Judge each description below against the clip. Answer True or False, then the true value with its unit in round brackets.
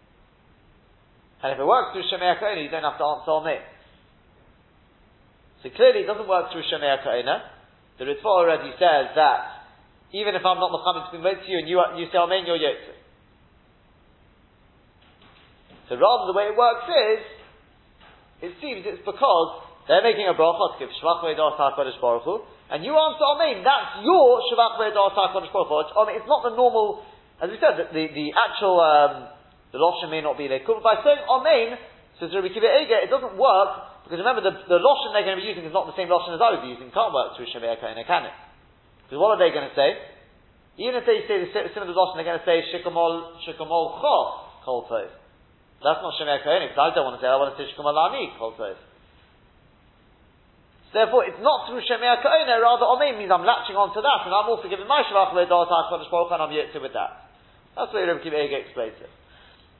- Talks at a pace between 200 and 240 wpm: True (205 wpm)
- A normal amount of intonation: False (7.3 semitones)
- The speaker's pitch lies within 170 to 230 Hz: True (185 Hz)